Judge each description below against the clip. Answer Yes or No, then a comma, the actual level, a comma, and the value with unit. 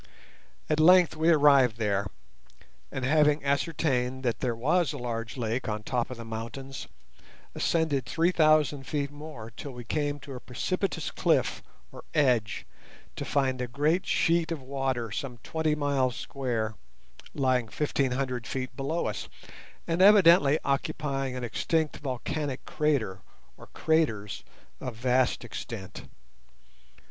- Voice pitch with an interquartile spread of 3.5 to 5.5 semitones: Yes, average, 3.8 semitones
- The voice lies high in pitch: No, low, 135 Hz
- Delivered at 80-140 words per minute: Yes, slow, 135 wpm